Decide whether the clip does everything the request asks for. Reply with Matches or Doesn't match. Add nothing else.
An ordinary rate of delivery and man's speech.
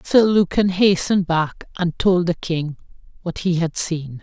Doesn't match